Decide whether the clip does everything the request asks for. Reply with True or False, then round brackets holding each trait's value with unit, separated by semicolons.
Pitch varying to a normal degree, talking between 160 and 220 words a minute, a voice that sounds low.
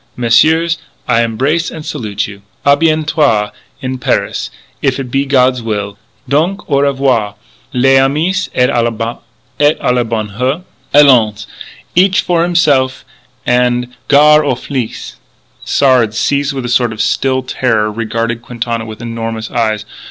False (3.7 semitones; 135 wpm; 125 Hz)